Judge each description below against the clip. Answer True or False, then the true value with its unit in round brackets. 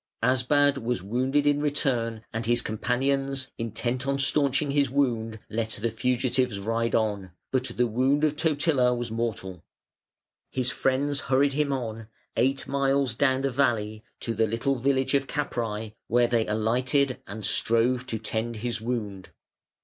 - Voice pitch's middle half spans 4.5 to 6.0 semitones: False (3.4 semitones)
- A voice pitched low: True (125 Hz)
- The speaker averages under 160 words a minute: True (150 wpm)